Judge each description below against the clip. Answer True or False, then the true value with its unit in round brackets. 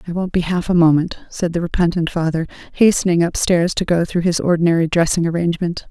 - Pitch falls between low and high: True (170 Hz)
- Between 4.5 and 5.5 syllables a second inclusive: False (6.1 syllables/s)